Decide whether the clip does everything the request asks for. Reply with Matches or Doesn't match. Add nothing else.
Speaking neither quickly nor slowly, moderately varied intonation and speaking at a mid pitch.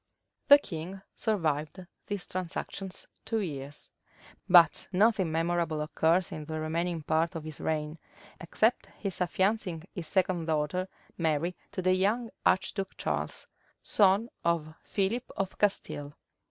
Doesn't match